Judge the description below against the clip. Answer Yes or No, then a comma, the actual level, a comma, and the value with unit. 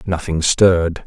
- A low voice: Yes, very low, 85 Hz